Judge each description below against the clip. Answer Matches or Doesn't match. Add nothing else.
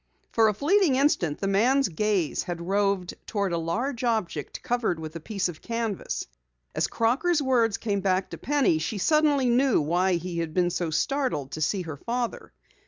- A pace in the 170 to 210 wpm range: Matches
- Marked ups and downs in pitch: Matches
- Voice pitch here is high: Matches